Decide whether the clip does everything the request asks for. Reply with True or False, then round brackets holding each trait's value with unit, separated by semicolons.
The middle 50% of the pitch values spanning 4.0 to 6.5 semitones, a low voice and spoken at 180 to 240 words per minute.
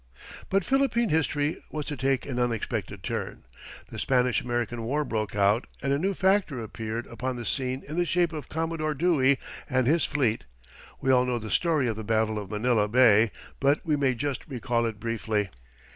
True (4.8 semitones; 130 Hz; 190 wpm)